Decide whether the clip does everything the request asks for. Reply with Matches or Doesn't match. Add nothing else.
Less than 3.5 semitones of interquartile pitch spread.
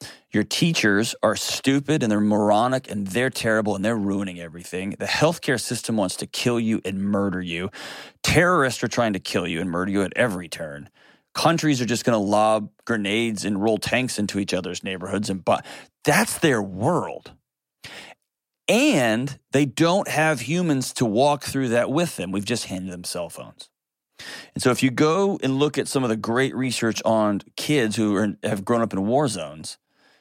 Doesn't match